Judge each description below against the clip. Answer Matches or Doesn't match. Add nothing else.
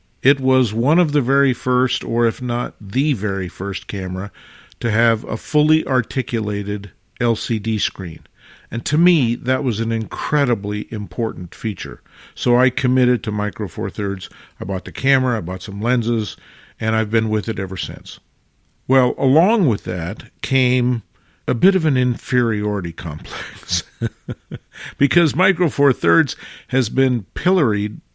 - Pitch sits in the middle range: Doesn't match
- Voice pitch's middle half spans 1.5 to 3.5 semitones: Doesn't match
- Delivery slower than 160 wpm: Matches